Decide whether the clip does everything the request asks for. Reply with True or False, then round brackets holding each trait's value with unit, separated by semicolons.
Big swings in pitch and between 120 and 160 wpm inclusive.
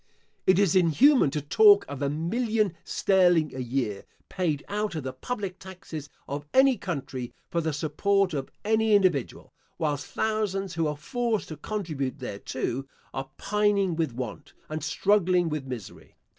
True (5.9 semitones; 155 wpm)